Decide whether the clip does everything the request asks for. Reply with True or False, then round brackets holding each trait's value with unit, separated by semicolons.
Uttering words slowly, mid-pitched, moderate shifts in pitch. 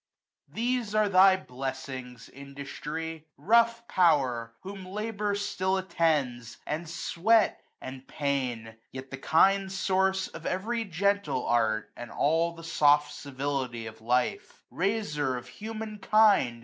False (125 wpm; 165 Hz; 7.4 semitones)